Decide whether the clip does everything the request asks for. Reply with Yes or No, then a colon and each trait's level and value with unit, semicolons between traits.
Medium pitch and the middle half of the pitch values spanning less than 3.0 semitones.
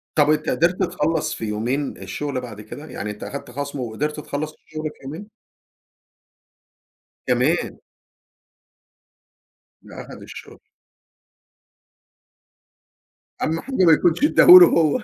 No: medium, 150 Hz; average, 4.5 semitones